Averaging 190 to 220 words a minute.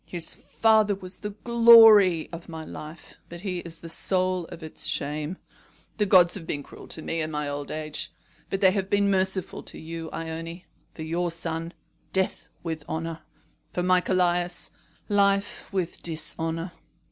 No: average, 165 wpm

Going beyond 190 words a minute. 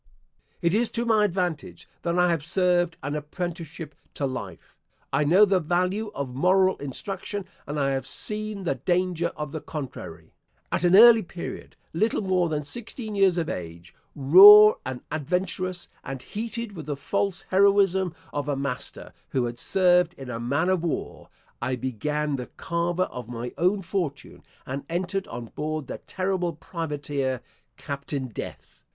No: average, 160 wpm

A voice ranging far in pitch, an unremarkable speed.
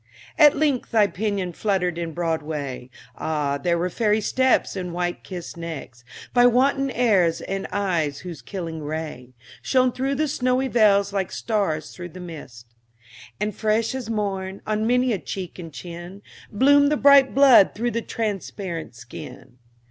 Yes: wide, 6.0 semitones; average, 155 wpm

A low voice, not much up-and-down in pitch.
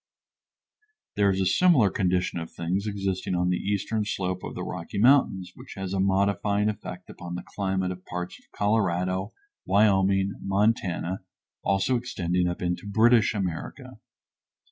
Yes: very low, 95 Hz; narrow, 2.1 semitones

